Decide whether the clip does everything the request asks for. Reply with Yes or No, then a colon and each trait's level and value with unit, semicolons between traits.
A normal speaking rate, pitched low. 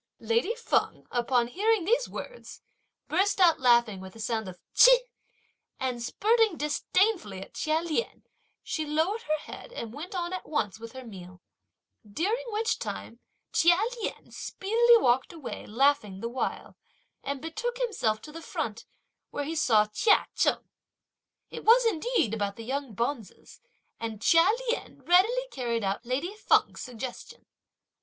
No: average, 150 wpm; very high, 295 Hz